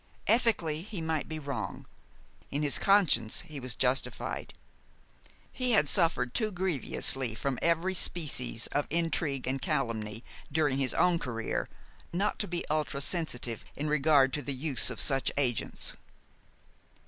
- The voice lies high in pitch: No, medium, 150 Hz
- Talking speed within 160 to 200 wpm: No, average, 140 wpm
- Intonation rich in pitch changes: No, average, 4.3 semitones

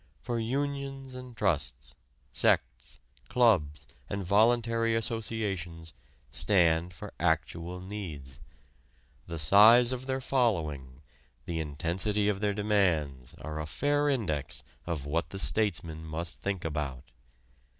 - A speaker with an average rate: No, slow, 115 wpm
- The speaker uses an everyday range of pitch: No, wide, 6.5 semitones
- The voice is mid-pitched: No, very low, 95 Hz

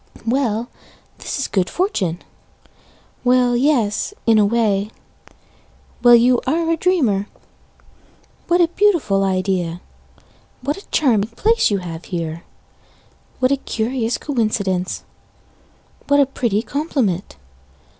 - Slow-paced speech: Yes, slow, 115 wpm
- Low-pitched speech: No, high, 235 Hz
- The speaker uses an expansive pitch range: Yes, wide, 6.1 semitones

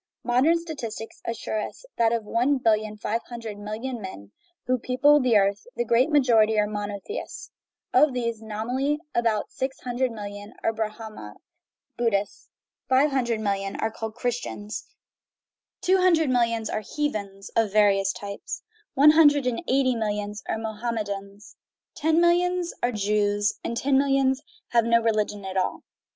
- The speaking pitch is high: Yes, high, 230 Hz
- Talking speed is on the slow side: No, average, 150 wpm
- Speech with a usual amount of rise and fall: Yes, average, 3.9 semitones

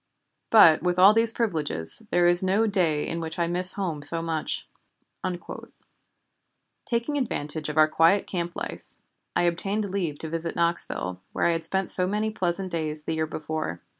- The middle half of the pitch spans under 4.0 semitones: Yes, average, 3.4 semitones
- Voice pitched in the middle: Yes, medium, 170 Hz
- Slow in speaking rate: No, average, 170 wpm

